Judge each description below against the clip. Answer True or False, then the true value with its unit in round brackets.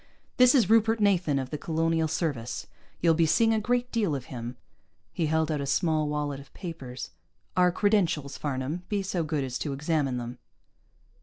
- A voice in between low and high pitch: True (160 Hz)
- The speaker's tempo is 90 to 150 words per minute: False (180 wpm)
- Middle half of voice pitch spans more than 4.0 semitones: True (5.2 semitones)